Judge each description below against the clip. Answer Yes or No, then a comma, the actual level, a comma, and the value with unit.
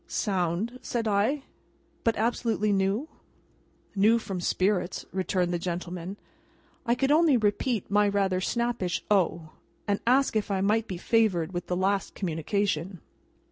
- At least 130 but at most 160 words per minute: Yes, average, 140 wpm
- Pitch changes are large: No, average, 3.8 semitones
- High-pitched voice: Yes, high, 200 Hz